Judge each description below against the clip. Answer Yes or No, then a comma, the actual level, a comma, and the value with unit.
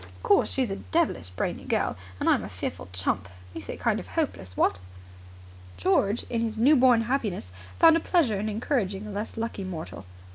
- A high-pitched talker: Yes, high, 205 Hz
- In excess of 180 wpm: Yes, average, 190 wpm